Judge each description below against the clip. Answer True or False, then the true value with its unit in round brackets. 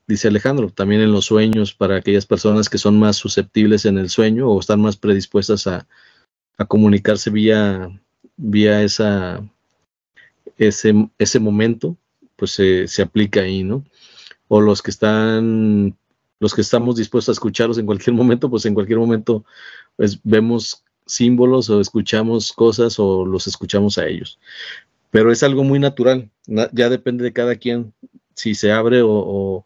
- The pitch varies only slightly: True (2.2 semitones)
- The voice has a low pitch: True (110 Hz)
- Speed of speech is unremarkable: True (160 wpm)